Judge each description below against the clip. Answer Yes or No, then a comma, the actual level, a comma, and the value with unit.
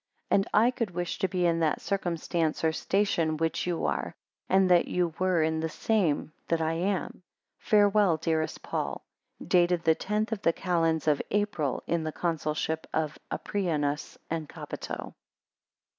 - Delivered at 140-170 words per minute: Yes, average, 160 wpm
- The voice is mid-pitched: Yes, medium, 170 Hz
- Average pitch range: Yes, average, 3.1 semitones